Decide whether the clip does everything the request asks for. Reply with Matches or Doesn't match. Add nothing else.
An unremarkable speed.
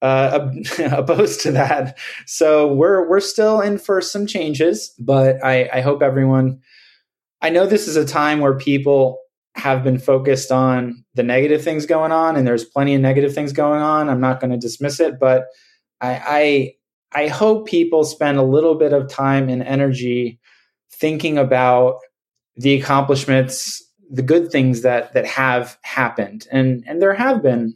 Matches